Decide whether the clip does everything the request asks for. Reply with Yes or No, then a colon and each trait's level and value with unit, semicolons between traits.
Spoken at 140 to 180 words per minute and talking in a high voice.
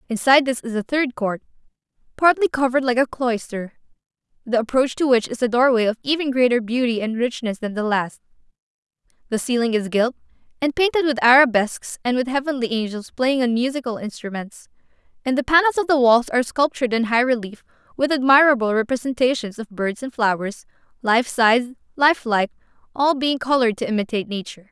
Yes: average, 170 wpm; high, 245 Hz